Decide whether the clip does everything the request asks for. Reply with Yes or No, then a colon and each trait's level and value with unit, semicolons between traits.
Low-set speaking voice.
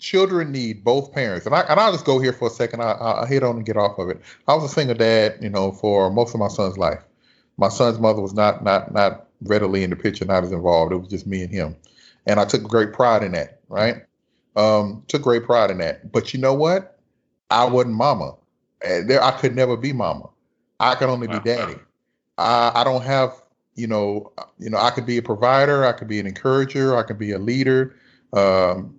Yes: low, 120 Hz